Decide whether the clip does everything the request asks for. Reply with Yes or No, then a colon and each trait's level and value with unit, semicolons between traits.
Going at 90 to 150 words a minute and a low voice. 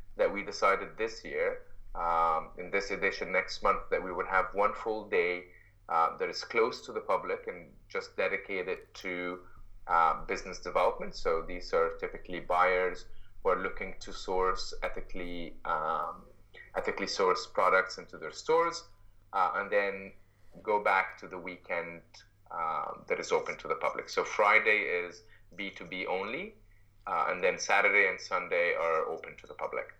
No: average, 160 wpm; low, 115 Hz